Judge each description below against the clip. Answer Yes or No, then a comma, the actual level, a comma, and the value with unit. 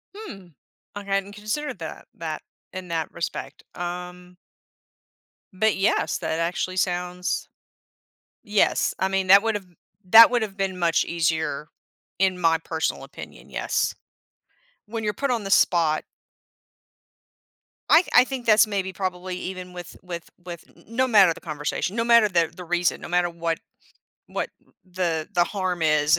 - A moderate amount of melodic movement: Yes, average, 3.1 semitones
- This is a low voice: No, medium, 180 Hz